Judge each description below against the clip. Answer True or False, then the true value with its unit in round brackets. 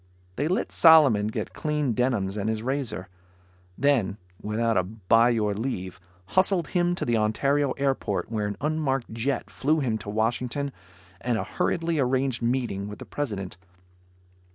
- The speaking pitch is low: True (120 Hz)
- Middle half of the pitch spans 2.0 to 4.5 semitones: False (4.9 semitones)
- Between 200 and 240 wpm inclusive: False (155 wpm)